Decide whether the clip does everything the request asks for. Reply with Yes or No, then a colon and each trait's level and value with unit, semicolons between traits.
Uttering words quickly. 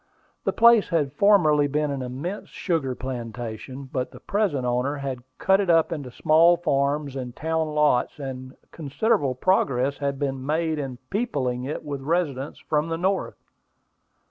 No: average, 155 wpm